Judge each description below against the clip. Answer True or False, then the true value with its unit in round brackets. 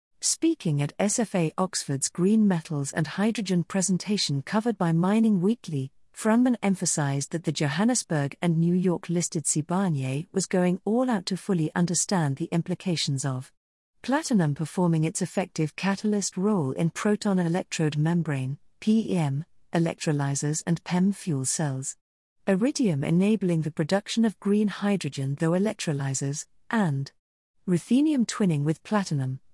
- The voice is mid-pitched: True (175 Hz)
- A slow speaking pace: True (125 wpm)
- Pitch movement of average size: True (5.0 semitones)